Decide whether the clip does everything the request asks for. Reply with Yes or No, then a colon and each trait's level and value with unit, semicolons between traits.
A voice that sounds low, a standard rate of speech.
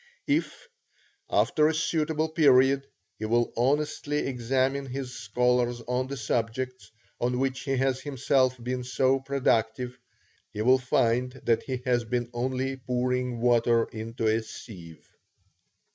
No: low, 125 Hz; slow, 130 wpm